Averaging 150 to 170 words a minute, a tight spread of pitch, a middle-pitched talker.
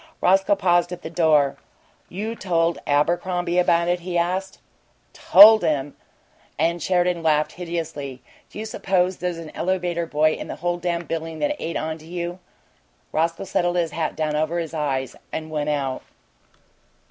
Yes: average, 160 wpm; narrow, 2.3 semitones; medium, 170 Hz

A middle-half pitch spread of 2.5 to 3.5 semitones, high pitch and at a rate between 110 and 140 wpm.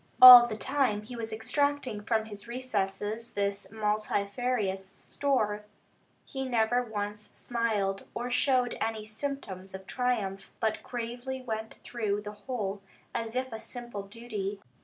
Yes: average, 3.1 semitones; high, 220 Hz; slow, 135 wpm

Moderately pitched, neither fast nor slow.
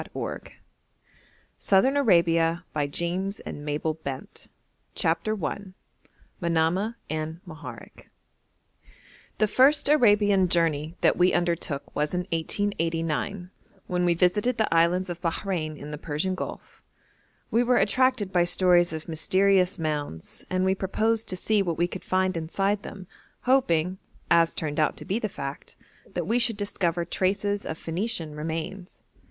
No: medium, 180 Hz; slow, 130 wpm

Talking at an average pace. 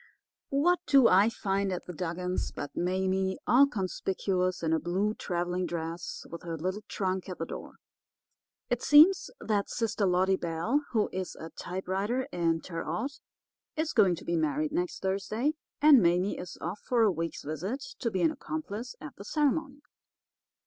Yes: average, 170 wpm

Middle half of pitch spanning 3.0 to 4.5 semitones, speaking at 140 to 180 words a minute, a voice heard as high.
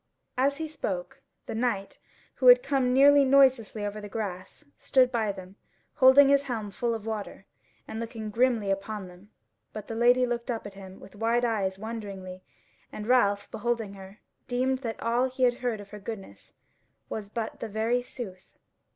Yes: average, 3.6 semitones; average, 175 wpm; high, 225 Hz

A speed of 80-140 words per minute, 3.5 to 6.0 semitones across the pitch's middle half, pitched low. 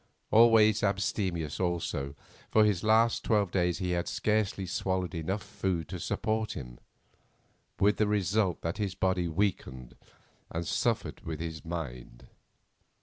Yes: slow, 135 wpm; average, 4.0 semitones; very low, 95 Hz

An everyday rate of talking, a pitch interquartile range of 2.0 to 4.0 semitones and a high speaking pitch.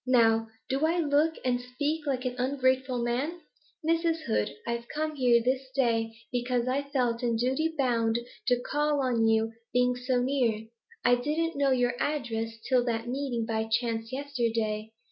Yes: average, 165 wpm; average, 3.2 semitones; very high, 250 Hz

